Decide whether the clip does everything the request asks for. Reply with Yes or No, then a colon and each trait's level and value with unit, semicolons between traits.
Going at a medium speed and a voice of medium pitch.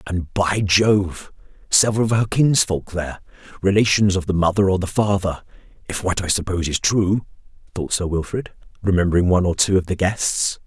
No: average, 175 wpm; very low, 95 Hz